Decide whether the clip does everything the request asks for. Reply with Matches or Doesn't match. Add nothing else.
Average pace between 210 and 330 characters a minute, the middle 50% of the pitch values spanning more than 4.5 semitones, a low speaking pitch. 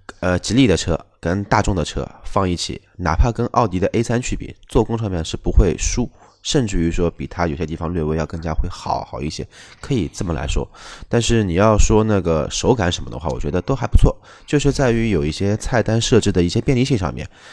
Matches